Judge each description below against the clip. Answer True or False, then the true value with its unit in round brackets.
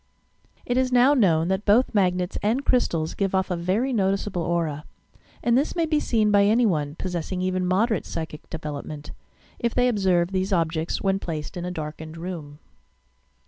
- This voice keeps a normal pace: True (175 wpm)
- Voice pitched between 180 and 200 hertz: True (185 Hz)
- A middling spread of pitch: True (4.7 semitones)